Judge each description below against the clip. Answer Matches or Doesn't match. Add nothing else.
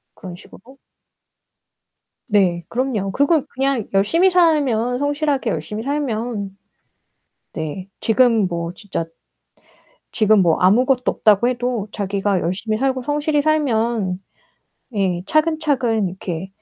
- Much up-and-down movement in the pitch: Matches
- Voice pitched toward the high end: Matches